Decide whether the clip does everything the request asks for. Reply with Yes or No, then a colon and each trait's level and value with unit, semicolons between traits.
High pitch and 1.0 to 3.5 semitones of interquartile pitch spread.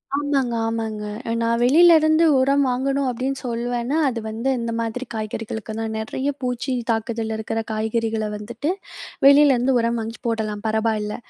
Yes: high, 235 Hz; average, 3.1 semitones